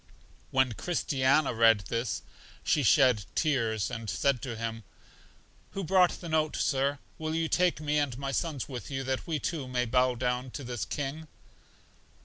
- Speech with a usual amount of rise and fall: Yes, average, 4.0 semitones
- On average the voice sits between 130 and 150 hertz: Yes, low, 135 Hz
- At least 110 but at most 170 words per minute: Yes, average, 165 wpm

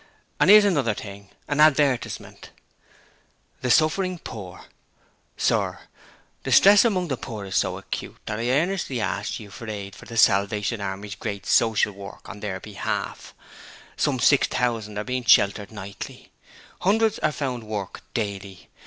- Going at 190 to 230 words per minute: No, average, 145 wpm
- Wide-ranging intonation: Yes, wide, 6.0 semitones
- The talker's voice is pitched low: Yes, low, 110 Hz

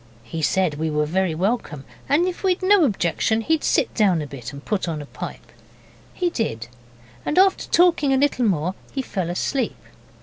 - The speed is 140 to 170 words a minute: No, average, 190 wpm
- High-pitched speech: Yes, high, 195 Hz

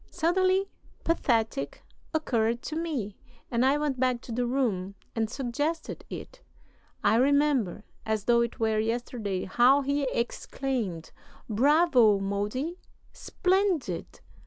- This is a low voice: No, high, 245 Hz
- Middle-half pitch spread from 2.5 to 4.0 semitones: No, average, 5.1 semitones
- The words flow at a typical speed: No, slow, 115 wpm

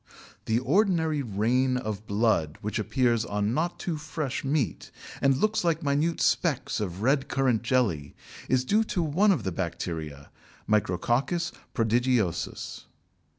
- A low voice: Yes, low, 125 Hz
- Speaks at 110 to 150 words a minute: Yes, slow, 135 wpm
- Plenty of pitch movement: Yes, wide, 6.4 semitones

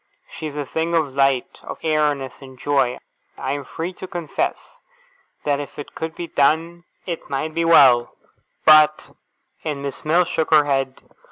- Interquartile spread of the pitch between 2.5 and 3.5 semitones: Yes, average, 2.8 semitones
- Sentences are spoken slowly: No, average, 175 wpm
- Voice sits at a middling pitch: Yes, medium, 150 Hz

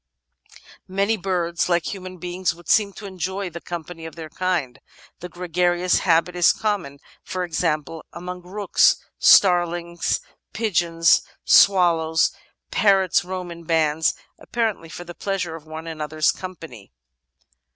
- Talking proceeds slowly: Yes, slow, 130 wpm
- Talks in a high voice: No, medium, 175 Hz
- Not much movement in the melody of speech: Yes, narrow, 2.2 semitones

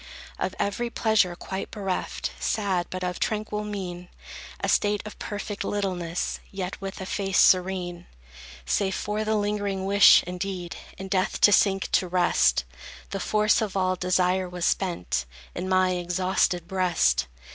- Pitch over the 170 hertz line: Yes, high, 190 Hz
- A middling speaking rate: Yes, average, 145 wpm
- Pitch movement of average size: No, narrow, 2.2 semitones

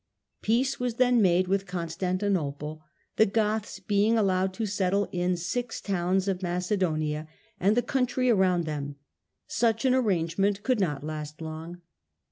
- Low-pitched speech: No, high, 190 Hz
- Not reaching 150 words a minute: Yes, average, 140 wpm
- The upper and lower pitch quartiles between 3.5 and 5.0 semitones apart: Yes, average, 4.3 semitones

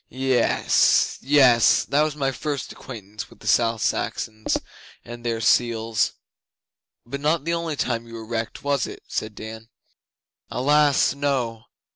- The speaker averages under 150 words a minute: Yes, average, 140 wpm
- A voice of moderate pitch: No, low, 120 Hz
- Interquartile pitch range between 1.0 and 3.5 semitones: No, average, 3.9 semitones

